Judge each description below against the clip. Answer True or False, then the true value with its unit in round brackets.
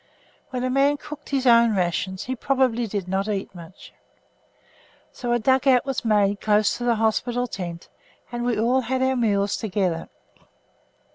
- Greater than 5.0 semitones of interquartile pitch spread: False (4.3 semitones)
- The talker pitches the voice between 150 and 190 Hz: False (230 Hz)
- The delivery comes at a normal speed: True (165 wpm)